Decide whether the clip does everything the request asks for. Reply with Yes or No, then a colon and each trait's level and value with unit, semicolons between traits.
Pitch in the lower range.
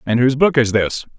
Yes: low, 125 Hz